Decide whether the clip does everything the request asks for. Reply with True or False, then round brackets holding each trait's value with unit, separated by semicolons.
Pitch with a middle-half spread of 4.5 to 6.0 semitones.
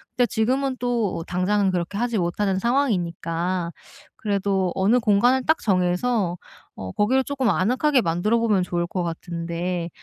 True (5.5 semitones)